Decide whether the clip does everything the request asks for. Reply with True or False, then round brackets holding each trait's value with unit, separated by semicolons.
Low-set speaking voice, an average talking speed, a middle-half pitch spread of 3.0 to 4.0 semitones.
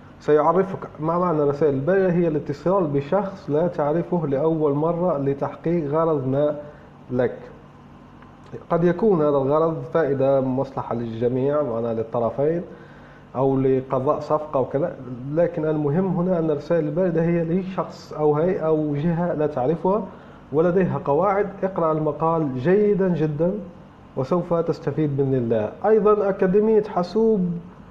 False (160 Hz; 125 wpm; 3.7 semitones)